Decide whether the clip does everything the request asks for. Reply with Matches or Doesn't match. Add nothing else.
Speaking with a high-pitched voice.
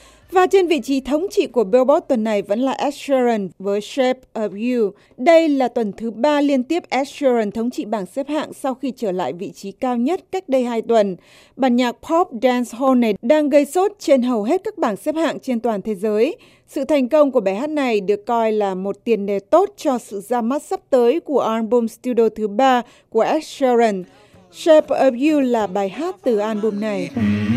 Matches